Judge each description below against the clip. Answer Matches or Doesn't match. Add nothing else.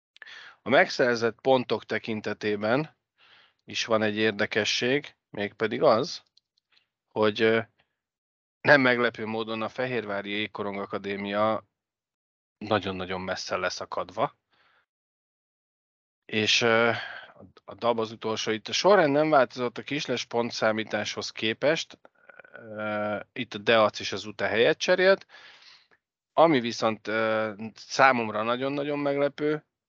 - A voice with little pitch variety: Matches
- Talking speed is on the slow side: Matches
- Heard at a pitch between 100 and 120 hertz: Matches